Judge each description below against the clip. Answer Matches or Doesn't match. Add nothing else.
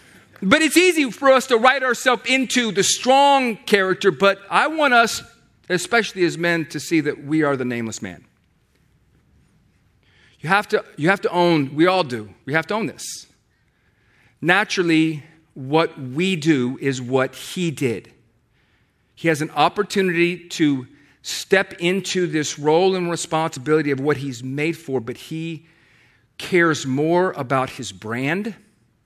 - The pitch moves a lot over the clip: Matches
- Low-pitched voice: Doesn't match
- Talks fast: Doesn't match